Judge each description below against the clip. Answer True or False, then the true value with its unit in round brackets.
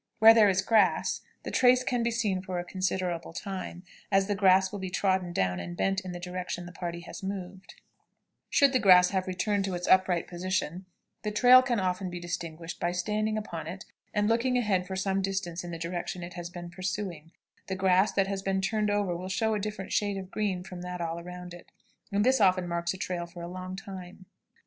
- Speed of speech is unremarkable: False (215 wpm)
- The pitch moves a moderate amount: False (2.3 semitones)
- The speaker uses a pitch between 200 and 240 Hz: False (185 Hz)